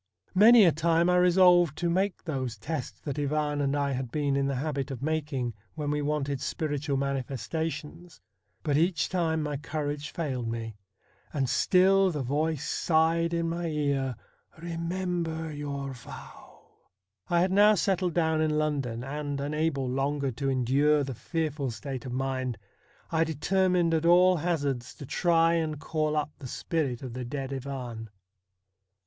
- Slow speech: No, average, 160 wpm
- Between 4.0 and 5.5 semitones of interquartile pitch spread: No, average, 3.4 semitones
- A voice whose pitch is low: No, medium, 150 Hz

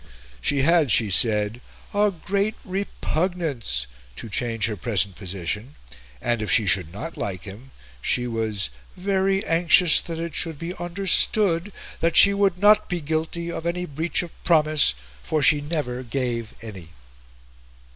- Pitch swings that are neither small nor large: No, wide, 7.9 semitones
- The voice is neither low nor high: Yes, medium, 150 Hz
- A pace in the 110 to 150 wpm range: Yes, average, 145 wpm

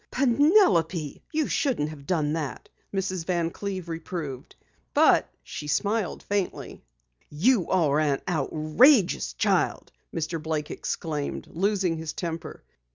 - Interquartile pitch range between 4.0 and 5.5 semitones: Yes, average, 4.4 semitones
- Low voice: No, medium, 165 Hz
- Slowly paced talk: Yes, slow, 115 wpm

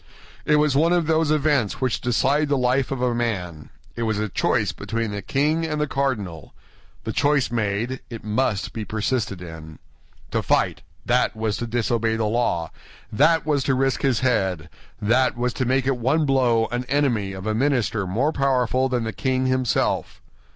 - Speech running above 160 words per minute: Yes, average, 180 wpm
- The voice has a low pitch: Yes, low, 125 Hz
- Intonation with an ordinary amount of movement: Yes, average, 3.9 semitones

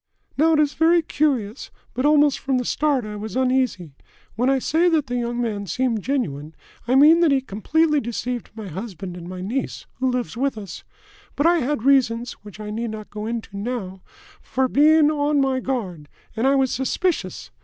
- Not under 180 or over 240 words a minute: Yes, average, 195 wpm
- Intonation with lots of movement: No, average, 5.0 semitones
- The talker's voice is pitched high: Yes, very high, 250 Hz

